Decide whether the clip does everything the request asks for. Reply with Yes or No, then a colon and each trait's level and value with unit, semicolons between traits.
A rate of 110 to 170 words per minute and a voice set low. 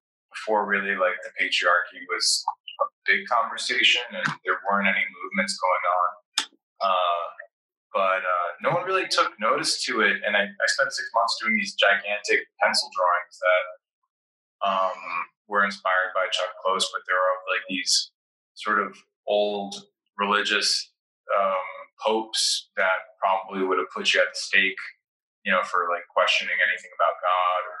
Yes: average, 160 wpm; low, 100 Hz